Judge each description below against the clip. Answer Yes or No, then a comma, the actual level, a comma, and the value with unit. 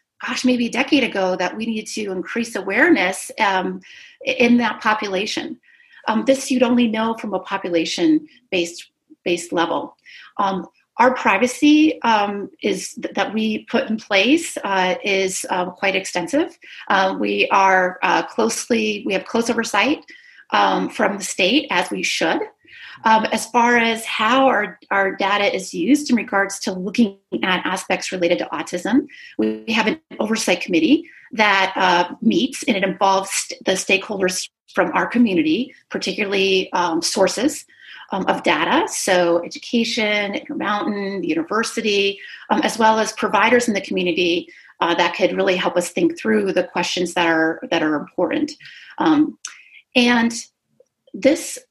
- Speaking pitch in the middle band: No, high, 220 Hz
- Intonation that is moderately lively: No, wide, 6.1 semitones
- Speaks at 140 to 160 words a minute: Yes, average, 150 wpm